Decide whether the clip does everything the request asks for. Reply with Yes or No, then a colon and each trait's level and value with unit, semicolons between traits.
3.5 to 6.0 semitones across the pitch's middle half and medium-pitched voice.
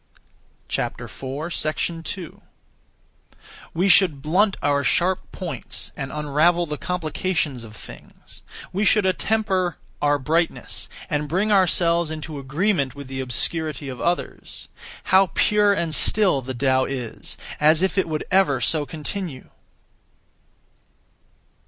Yes: average, 4.6 semitones; medium, 160 Hz